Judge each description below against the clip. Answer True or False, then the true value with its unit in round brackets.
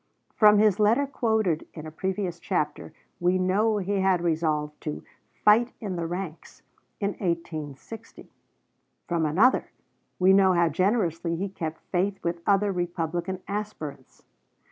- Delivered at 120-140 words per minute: True (135 wpm)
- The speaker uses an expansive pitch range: False (3.4 semitones)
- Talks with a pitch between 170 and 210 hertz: True (185 Hz)